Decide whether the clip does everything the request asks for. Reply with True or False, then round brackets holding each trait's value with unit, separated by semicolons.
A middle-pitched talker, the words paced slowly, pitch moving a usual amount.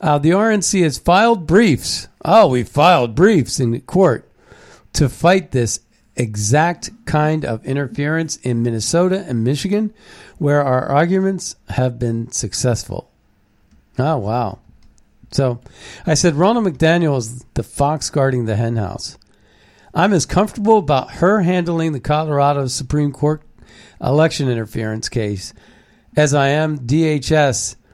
False (145 Hz; 130 wpm; 5.8 semitones)